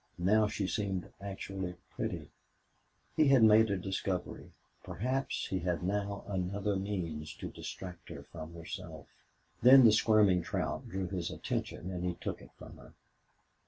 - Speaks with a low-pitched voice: Yes, very low, 95 Hz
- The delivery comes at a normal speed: Yes, average, 150 wpm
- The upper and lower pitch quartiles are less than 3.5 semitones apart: Yes, average, 2.8 semitones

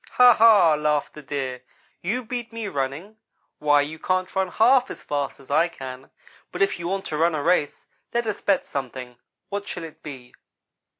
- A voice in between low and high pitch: Yes, medium, 165 Hz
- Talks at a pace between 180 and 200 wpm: Yes, average, 190 wpm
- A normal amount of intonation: No, wide, 6.1 semitones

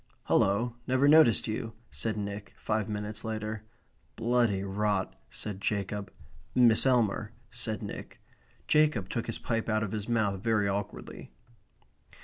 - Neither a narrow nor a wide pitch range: No, narrow, 2.3 semitones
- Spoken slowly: Yes, slow, 130 wpm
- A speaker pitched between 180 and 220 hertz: No, low, 110 Hz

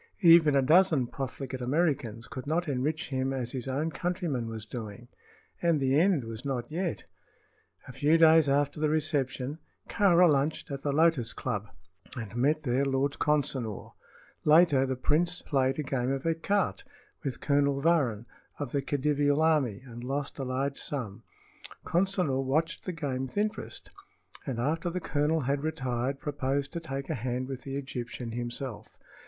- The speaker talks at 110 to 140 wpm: No, average, 160 wpm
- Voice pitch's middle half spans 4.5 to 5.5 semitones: No, average, 3.6 semitones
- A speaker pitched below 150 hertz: Yes, medium, 140 Hz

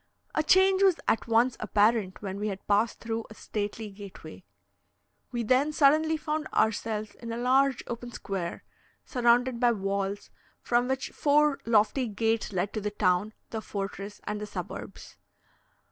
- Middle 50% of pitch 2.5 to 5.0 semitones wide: Yes, average, 3.8 semitones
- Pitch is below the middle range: No, high, 225 Hz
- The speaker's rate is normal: Yes, average, 155 wpm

